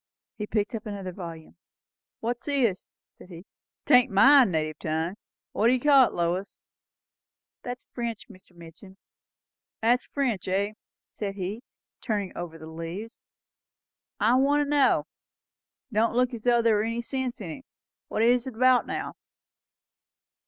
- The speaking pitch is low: No, high, 220 Hz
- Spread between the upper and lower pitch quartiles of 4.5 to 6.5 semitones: Yes, average, 5.1 semitones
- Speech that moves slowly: No, average, 155 wpm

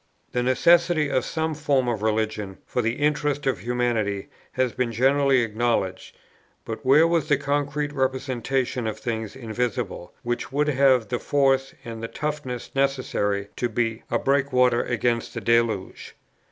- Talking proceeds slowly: No, average, 150 wpm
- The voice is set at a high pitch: No, low, 125 Hz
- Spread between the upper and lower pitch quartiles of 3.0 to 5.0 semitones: Yes, average, 3.4 semitones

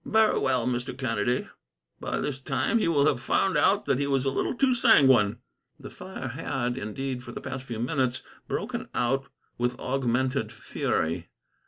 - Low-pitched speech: Yes, low, 130 Hz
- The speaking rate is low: No, average, 170 wpm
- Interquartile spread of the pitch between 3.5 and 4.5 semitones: No, narrow, 2.5 semitones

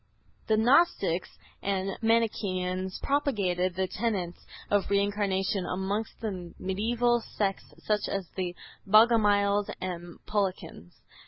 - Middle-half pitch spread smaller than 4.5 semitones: Yes, average, 2.7 semitones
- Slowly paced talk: Yes, slow, 100 wpm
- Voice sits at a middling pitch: No, high, 200 Hz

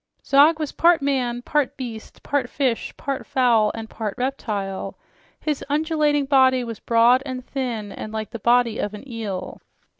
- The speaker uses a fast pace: No, average, 160 wpm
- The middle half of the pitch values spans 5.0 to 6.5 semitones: No, average, 3.7 semitones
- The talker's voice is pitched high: Yes, very high, 250 Hz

